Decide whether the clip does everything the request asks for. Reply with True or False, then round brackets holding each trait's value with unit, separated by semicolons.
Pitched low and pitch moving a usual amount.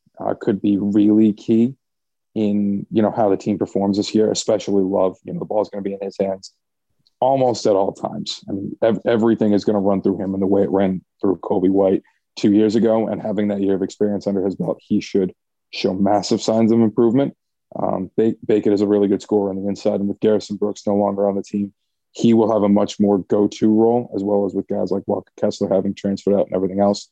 False (100 Hz; 1.5 semitones)